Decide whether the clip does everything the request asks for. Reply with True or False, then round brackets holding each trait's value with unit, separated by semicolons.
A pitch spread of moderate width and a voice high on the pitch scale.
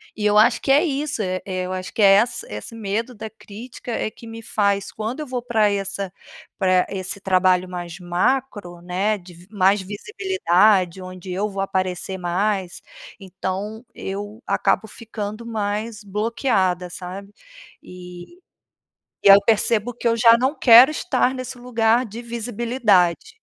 True (3.8 semitones; 205 Hz)